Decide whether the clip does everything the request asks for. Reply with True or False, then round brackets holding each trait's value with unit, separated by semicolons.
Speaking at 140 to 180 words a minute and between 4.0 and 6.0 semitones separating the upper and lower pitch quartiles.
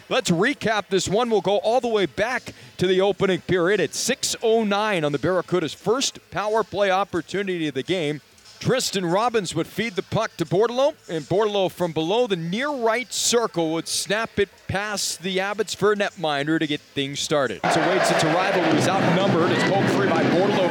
False (195 wpm; 4.4 semitones)